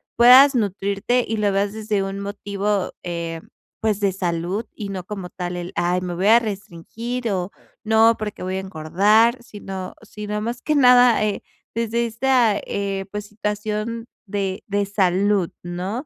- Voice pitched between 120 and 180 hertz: No, high, 205 Hz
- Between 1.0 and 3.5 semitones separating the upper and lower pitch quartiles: Yes, average, 2.9 semitones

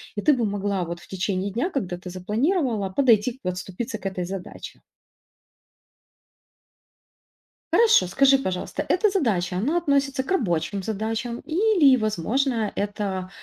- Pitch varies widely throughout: Yes, wide, 6.4 semitones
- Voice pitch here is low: No, high, 215 Hz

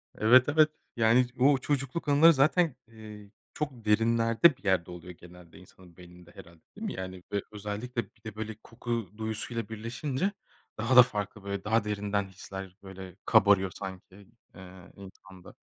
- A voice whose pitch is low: Yes, low, 105 Hz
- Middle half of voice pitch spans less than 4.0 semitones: No, average, 4.3 semitones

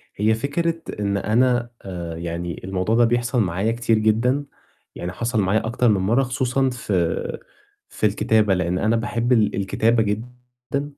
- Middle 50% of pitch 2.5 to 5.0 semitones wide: Yes, average, 3.9 semitones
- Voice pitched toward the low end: Yes, low, 110 Hz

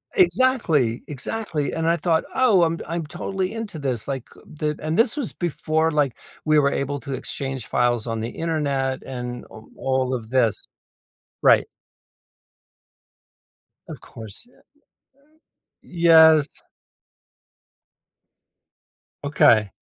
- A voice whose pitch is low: No, medium, 150 Hz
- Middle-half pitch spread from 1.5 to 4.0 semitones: No, average, 4.6 semitones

